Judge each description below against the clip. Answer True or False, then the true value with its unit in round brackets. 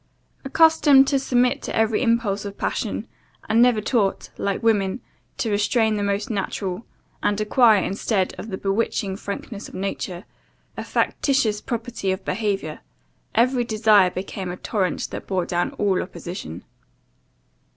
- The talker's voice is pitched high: True (210 Hz)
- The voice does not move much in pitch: False (3.2 semitones)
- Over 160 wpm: False (140 wpm)